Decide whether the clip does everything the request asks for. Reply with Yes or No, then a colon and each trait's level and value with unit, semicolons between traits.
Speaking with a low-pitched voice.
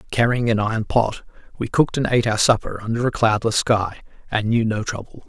Yes: low, 110 Hz